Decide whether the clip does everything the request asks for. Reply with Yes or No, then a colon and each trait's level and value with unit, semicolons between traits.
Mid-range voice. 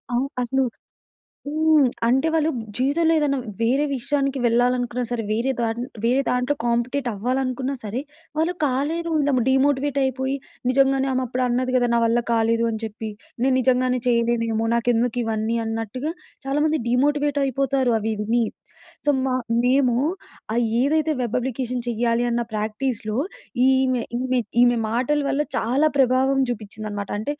No: very high, 255 Hz